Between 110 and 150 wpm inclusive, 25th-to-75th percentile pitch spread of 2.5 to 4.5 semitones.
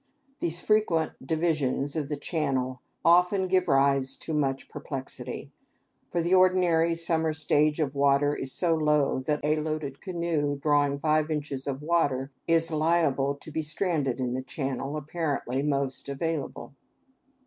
Yes: average, 145 wpm; average, 3.0 semitones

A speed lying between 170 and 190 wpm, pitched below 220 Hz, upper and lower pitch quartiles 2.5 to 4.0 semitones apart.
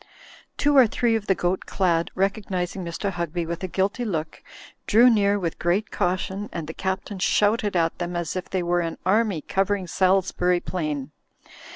Yes: average, 185 wpm; medium, 185 Hz; average, 2.8 semitones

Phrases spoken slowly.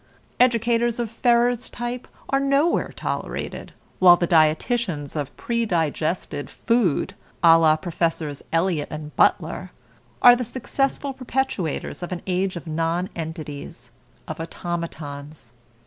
Yes: slow, 115 wpm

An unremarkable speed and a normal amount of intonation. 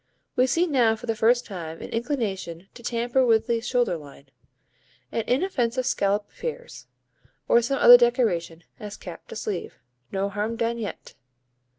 Yes: average, 160 wpm; average, 3.6 semitones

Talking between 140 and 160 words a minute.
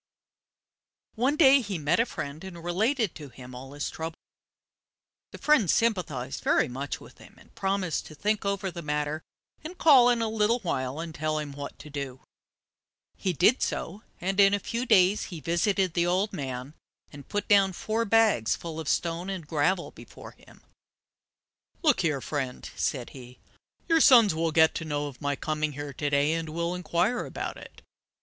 No: average, 180 wpm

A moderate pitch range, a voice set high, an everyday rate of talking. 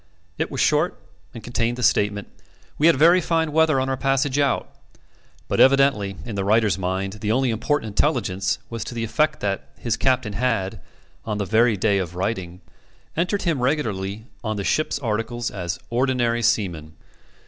No: average, 5.0 semitones; low, 115 Hz; average, 170 wpm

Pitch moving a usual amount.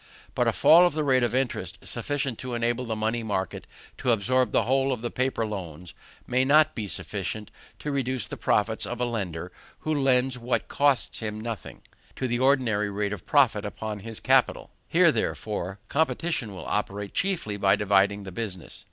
Yes: average, 4.2 semitones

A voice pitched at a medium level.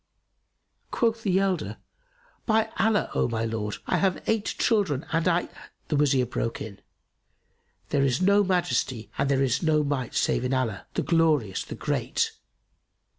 Yes: medium, 145 Hz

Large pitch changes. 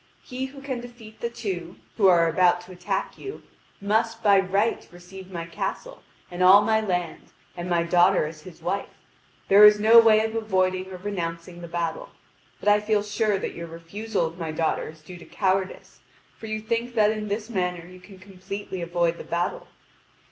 No: average, 3.6 semitones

